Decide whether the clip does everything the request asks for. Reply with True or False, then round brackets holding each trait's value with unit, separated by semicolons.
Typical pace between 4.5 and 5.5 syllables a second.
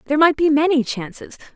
False (6.6 syllables/s)